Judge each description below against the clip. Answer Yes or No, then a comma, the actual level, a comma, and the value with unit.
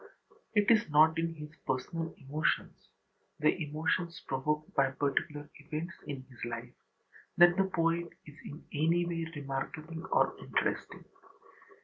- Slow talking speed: Yes, slow, 130 wpm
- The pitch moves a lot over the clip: No, average, 2.7 semitones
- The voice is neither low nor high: Yes, medium, 155 Hz